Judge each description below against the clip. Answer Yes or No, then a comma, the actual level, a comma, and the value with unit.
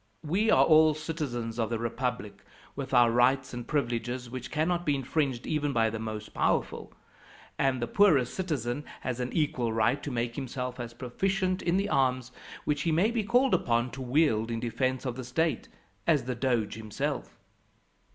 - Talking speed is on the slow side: No, average, 180 wpm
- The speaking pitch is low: Yes, low, 130 Hz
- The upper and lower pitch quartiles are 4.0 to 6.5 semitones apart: Yes, average, 4.5 semitones